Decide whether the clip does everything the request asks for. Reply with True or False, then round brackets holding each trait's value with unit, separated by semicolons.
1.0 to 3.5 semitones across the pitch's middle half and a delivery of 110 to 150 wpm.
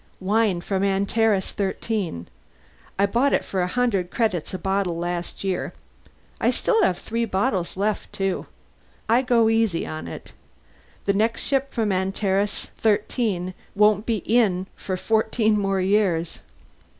True (3.1 semitones; 140 wpm)